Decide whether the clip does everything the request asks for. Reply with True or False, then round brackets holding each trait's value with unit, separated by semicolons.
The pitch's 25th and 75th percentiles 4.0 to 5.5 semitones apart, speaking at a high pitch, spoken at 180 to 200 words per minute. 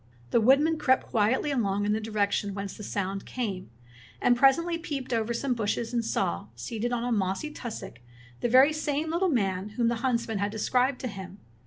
True (4.4 semitones; 235 Hz; 190 wpm)